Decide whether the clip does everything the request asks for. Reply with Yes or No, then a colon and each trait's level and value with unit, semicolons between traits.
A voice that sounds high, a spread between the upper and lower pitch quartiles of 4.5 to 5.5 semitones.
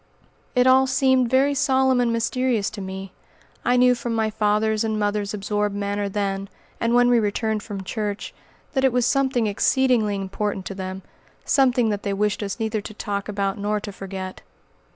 No: high, 215 Hz; average, 3.6 semitones